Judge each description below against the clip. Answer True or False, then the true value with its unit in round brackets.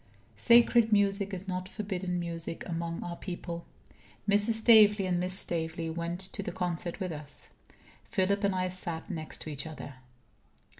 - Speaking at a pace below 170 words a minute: True (155 wpm)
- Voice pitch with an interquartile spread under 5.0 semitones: True (3.0 semitones)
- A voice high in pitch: False (180 Hz)